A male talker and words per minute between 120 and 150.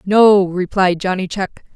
No: female; slow, 135 wpm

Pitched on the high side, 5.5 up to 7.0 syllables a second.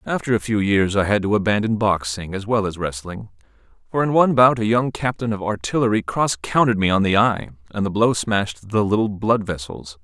No: low, 105 Hz; 5.7 syllables/s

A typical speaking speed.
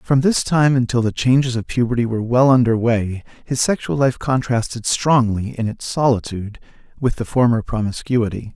Yes: average, 170 wpm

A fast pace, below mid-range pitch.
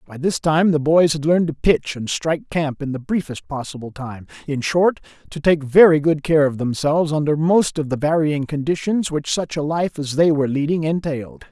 No: fast, 210 wpm; medium, 150 Hz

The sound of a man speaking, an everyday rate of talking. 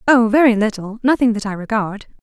No: female; average, 190 wpm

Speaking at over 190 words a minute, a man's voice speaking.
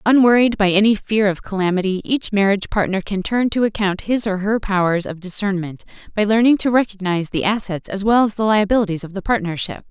No: average, 200 wpm; female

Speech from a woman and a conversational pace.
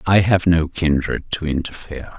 No: male; average, 165 wpm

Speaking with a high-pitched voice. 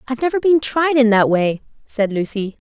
Yes: high, 245 Hz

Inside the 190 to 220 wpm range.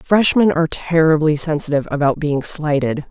No: slow, 135 wpm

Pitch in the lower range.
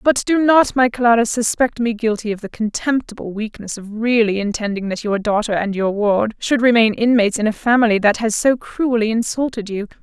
No: high, 225 Hz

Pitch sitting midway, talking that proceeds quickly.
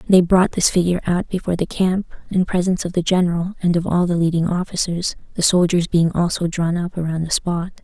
Yes: medium, 175 Hz; fast, 215 wpm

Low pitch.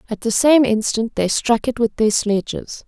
No: high, 230 Hz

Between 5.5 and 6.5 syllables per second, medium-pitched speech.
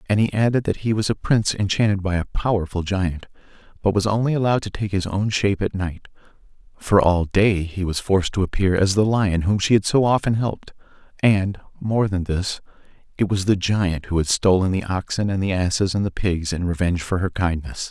No: 5.6 syllables/s; very low, 95 Hz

